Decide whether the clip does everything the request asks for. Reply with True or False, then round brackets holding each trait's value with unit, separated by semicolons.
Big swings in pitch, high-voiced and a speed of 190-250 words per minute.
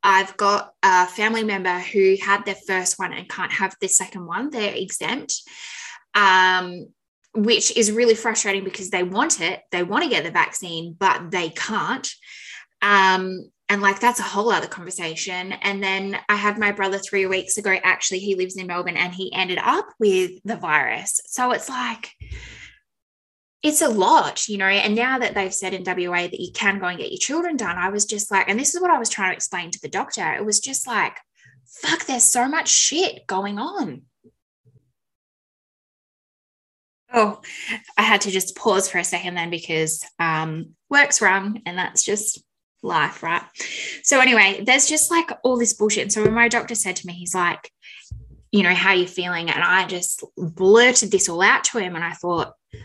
False (3.9 semitones; 195 Hz; 195 wpm)